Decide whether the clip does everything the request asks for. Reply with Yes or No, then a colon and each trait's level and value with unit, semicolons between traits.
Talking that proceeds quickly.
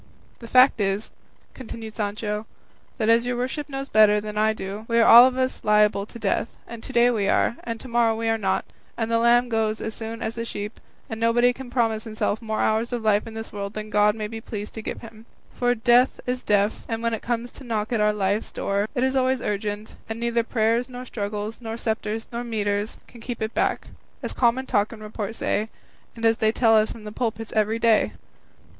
Yes: fast, 225 wpm